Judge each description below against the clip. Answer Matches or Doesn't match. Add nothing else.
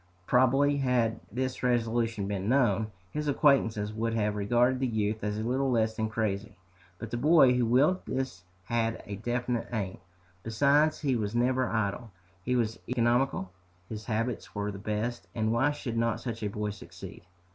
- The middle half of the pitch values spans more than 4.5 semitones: Doesn't match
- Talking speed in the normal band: Matches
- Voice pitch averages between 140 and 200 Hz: Doesn't match